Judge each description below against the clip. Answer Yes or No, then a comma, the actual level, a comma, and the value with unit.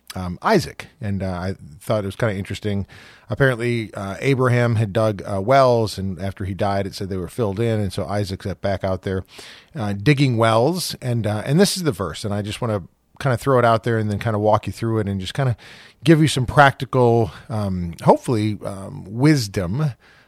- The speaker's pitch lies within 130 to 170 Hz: No, low, 110 Hz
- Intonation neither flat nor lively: Yes, average, 3.9 semitones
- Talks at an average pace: No, fast, 225 wpm